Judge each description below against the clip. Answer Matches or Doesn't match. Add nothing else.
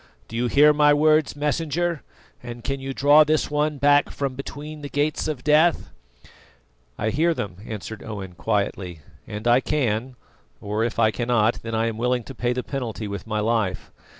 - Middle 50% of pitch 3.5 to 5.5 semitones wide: Matches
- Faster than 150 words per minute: Matches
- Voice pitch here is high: Doesn't match